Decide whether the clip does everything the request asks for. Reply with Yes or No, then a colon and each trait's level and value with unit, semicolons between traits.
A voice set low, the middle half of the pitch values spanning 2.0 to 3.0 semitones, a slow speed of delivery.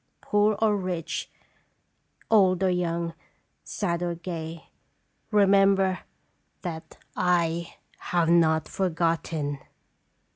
No: medium, 175 Hz; narrow, 2.5 semitones; slow, 95 wpm